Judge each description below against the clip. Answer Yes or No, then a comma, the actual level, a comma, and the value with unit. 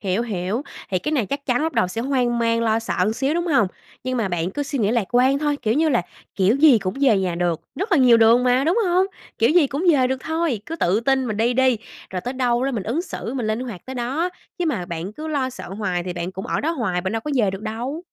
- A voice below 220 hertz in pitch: No, high, 240 Hz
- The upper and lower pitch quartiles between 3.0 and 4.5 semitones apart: No, average, 5.3 semitones